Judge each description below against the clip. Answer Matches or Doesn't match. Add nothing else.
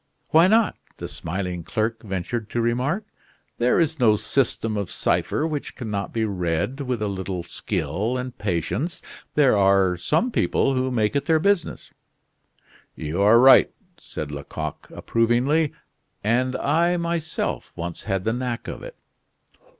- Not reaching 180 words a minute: Matches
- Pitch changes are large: Matches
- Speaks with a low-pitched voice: Matches